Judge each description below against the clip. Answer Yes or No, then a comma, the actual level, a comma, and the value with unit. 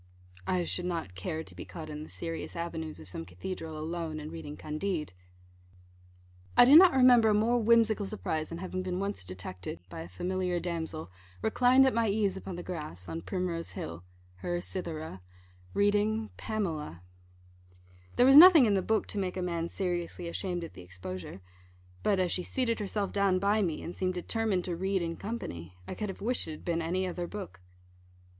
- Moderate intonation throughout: Yes, average, 4.4 semitones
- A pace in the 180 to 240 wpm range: Yes, average, 190 wpm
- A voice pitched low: No, medium, 180 Hz